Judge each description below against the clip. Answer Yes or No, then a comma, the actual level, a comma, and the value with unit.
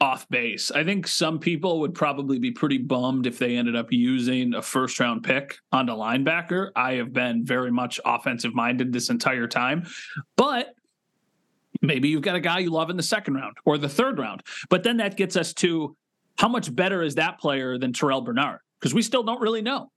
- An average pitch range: No, wide, 6.6 semitones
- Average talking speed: No, fast, 210 wpm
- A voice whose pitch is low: No, medium, 155 Hz